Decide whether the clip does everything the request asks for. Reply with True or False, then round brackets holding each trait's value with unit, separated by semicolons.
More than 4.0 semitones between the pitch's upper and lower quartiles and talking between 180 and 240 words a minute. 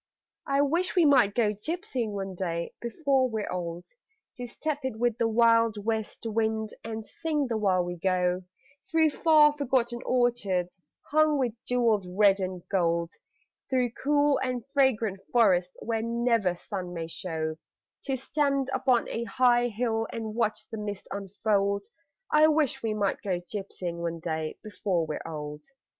False (5.3 semitones; 155 wpm)